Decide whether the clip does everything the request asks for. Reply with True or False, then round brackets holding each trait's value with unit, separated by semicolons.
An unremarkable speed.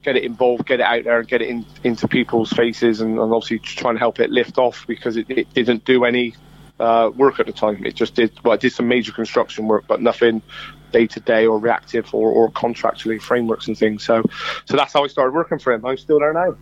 False (255 wpm)